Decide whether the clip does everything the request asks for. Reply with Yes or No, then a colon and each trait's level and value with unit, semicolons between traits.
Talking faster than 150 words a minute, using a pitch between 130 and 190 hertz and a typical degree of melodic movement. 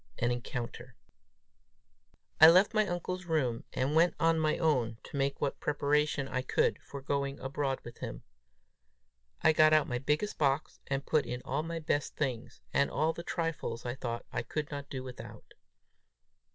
Yes: average, 170 wpm; medium, 140 Hz; average, 3.5 semitones